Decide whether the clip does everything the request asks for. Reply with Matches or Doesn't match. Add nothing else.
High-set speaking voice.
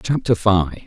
Doesn't match